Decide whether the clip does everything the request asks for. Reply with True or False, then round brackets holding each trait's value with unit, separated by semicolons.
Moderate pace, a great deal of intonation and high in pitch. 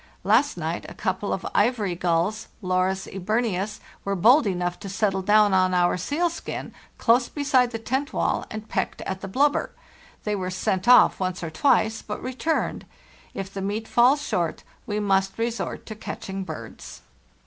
False (160 wpm; 4.0 semitones; 205 Hz)